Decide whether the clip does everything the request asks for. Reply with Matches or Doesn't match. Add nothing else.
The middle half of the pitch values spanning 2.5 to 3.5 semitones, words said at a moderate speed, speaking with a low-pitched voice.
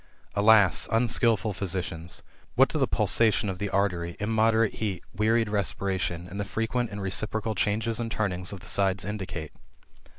Matches